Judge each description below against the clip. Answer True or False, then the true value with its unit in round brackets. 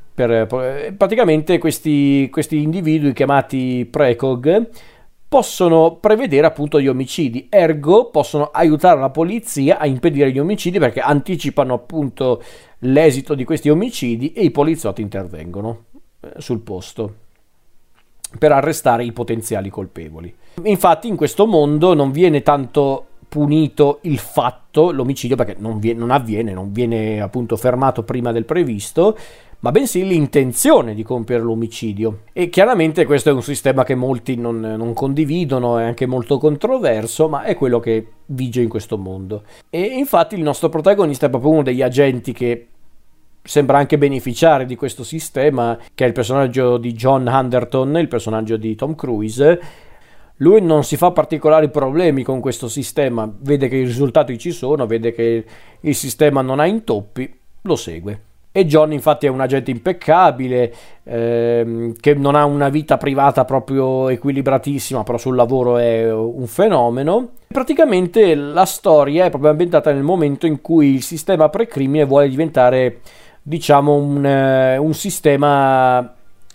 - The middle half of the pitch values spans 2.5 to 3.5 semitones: False (4.3 semitones)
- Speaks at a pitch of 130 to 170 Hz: True (135 Hz)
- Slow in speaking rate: False (145 wpm)